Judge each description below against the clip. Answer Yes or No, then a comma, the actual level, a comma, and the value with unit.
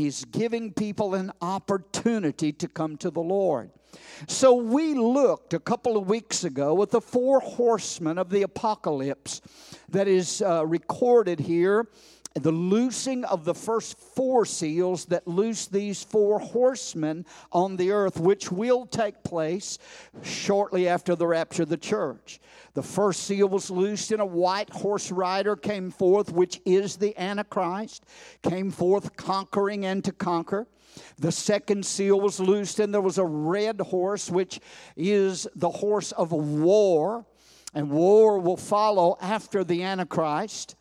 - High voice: Yes, high, 195 Hz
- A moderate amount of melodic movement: Yes, average, 3.2 semitones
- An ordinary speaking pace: Yes, average, 150 wpm